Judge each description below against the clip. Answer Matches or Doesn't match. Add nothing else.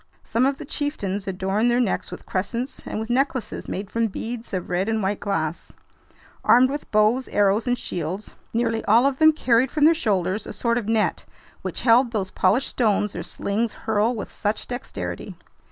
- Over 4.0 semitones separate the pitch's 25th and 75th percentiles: Doesn't match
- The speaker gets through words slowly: Doesn't match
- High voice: Matches